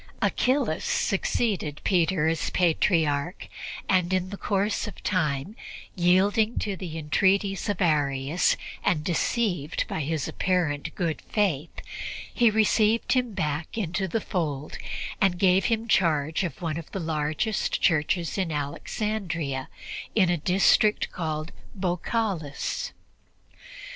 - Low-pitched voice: No, medium, 180 Hz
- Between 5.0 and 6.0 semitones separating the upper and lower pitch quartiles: No, average, 4.4 semitones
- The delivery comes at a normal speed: No, slow, 120 wpm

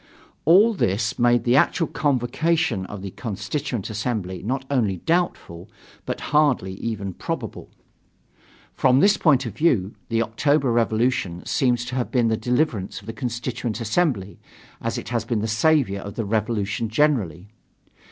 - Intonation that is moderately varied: Yes, average, 4.4 semitones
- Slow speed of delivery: No, average, 150 wpm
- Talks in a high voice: No, low, 115 Hz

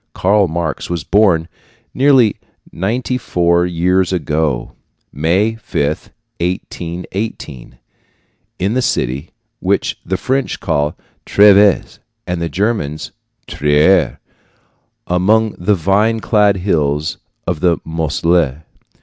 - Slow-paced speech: Yes, slow, 100 wpm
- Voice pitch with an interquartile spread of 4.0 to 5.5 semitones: Yes, average, 4.5 semitones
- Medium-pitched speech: No, very low, 90 Hz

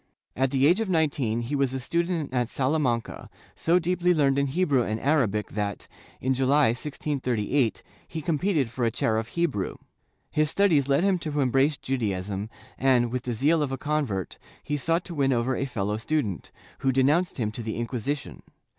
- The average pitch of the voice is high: No, low, 135 Hz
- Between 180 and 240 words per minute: Yes, average, 190 wpm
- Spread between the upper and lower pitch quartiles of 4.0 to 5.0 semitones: Yes, average, 4.5 semitones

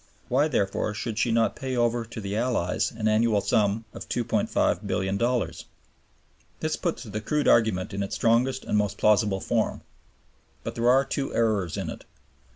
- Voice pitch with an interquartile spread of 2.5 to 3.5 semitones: Yes, average, 2.9 semitones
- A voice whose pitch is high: No, low, 115 Hz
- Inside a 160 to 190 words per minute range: Yes, average, 165 wpm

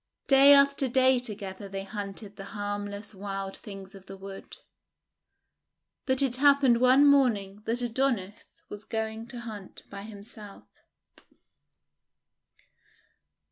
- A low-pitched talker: No, high, 215 Hz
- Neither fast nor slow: No, slow, 120 wpm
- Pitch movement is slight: No, average, 4.3 semitones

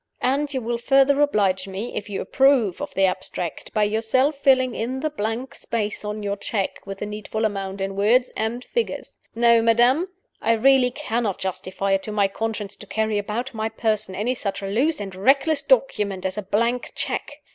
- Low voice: No, high, 220 Hz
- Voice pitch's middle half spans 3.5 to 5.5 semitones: Yes, average, 4.1 semitones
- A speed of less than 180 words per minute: No, average, 190 wpm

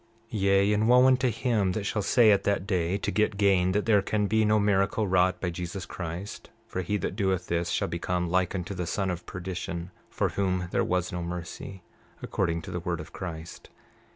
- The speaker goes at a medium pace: No, fast, 210 wpm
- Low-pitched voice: Yes, very low, 95 Hz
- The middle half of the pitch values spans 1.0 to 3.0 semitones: Yes, narrow, 2.6 semitones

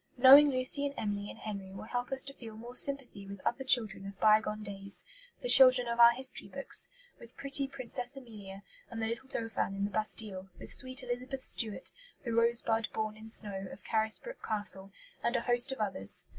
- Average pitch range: Yes, average, 3.7 semitones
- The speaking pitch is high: Yes, high, 230 Hz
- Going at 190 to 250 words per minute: Yes, average, 200 wpm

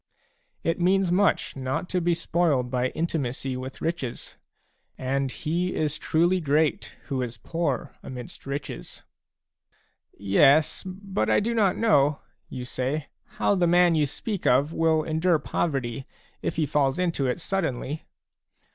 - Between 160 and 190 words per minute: No, average, 145 wpm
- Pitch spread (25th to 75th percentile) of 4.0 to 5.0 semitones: Yes, average, 4.7 semitones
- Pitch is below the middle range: No, medium, 155 Hz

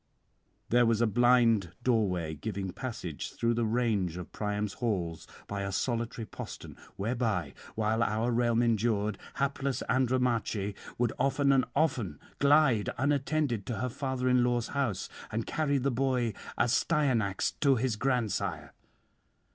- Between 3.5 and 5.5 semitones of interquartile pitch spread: Yes, average, 3.8 semitones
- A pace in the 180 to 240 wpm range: No, slow, 135 wpm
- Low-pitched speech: Yes, low, 115 Hz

